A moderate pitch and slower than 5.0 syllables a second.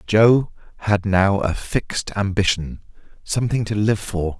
No: low, 100 Hz; 4.3 syllables/s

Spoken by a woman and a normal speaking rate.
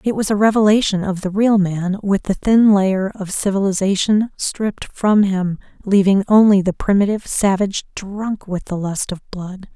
Yes: female; average, 170 wpm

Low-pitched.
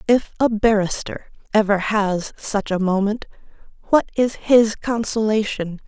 No: high, 210 Hz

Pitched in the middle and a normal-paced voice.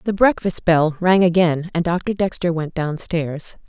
Yes: medium, 170 Hz; average, 165 wpm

